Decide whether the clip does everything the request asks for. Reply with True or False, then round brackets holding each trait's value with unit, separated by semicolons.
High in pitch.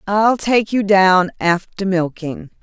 True (195 Hz)